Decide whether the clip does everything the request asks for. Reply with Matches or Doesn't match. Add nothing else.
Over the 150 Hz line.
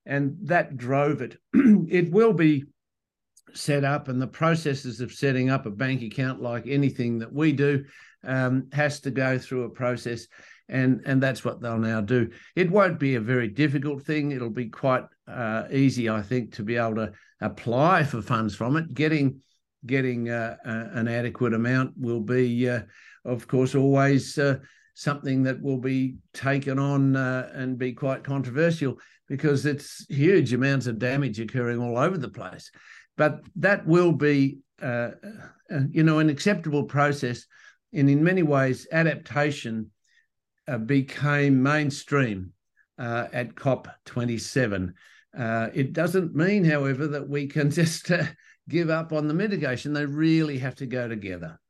Doesn't match